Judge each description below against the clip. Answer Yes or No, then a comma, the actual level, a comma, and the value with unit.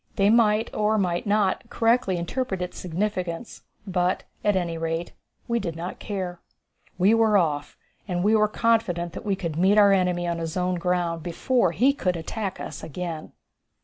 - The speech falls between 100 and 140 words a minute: No, average, 170 wpm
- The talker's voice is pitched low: No, medium, 185 Hz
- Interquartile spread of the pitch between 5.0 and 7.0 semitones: No, average, 3.5 semitones